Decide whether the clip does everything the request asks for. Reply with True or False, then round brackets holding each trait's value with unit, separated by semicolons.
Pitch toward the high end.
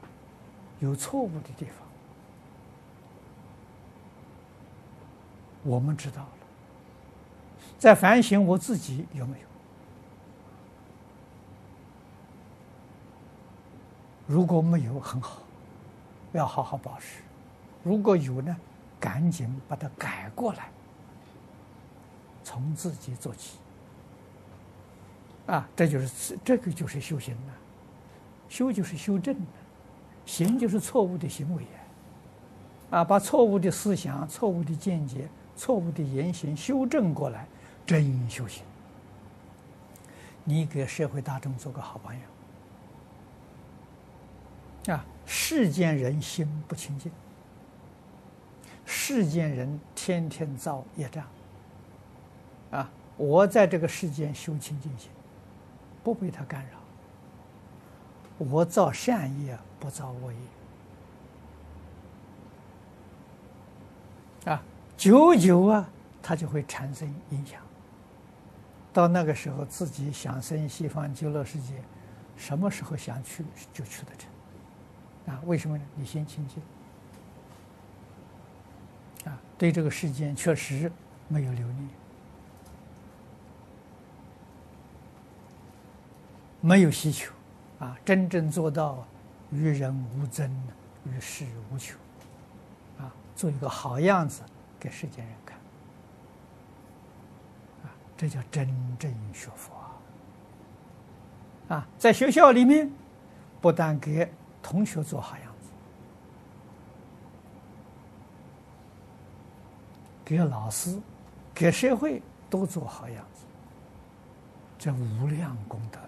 False (140 Hz)